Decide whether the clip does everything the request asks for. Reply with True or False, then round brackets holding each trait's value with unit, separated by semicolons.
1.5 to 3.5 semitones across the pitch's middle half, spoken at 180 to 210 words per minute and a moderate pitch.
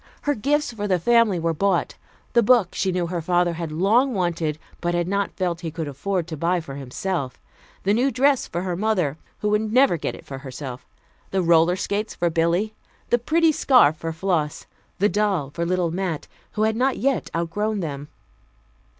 False (4.6 semitones; 195 wpm; 180 Hz)